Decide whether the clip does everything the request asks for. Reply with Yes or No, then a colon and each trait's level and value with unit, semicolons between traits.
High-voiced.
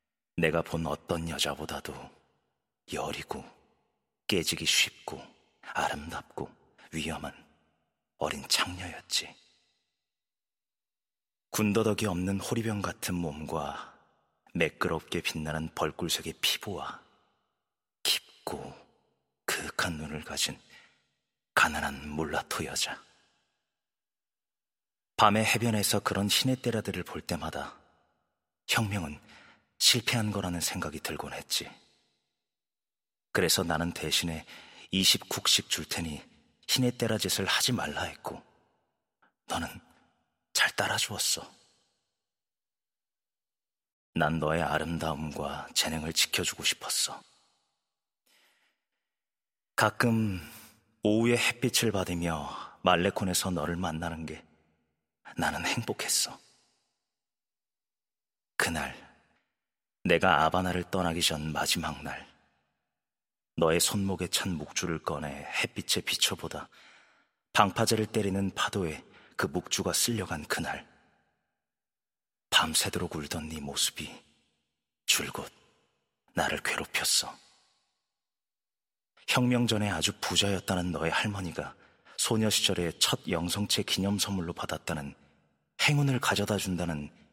No: very low, 90 Hz